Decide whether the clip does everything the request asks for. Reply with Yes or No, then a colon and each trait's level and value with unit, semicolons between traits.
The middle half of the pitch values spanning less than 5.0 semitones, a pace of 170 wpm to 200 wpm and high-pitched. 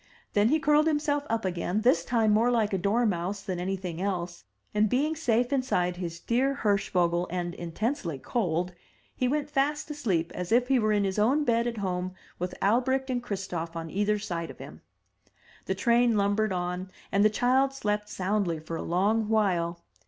No: wide, 5.4 semitones; average, 180 wpm; high, 210 Hz